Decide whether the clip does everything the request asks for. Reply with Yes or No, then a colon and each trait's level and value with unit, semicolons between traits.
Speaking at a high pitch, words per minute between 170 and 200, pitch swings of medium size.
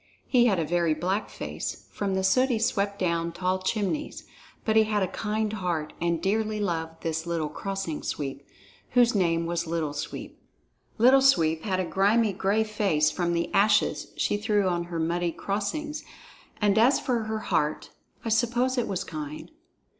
Yes: high, 195 Hz; average, 175 wpm; average, 4.5 semitones